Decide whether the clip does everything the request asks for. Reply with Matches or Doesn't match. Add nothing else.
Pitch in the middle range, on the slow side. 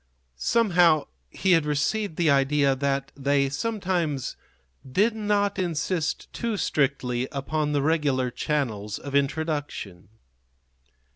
Matches